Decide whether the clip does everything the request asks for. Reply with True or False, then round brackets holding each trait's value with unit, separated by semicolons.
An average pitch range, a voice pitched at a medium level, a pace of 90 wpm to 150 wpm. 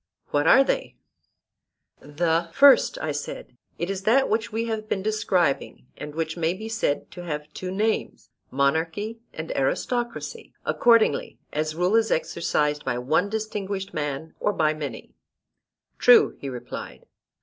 False (6.4 semitones; 175 Hz; 140 wpm)